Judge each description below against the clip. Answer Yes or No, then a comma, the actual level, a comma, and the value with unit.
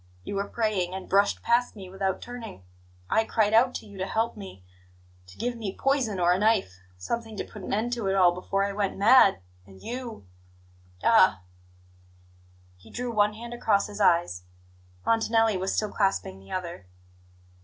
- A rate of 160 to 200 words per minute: Yes, average, 180 wpm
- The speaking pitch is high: Yes, high, 200 Hz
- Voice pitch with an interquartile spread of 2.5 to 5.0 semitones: Yes, average, 4.0 semitones